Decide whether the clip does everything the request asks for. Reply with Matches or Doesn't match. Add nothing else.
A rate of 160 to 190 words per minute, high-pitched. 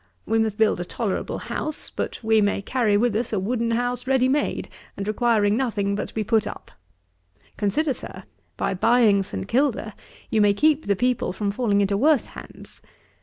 Matches